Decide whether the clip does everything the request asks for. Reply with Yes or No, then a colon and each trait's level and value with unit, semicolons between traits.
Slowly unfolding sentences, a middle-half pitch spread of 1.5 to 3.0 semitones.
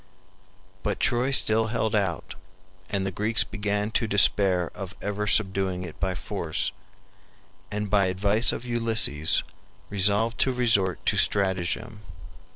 Yes: slow, 130 wpm; narrow, 2.6 semitones